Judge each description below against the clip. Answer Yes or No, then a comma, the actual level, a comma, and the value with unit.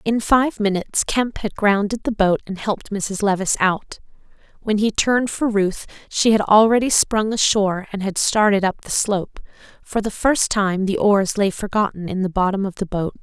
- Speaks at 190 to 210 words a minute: Yes, average, 195 wpm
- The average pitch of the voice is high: Yes, high, 205 Hz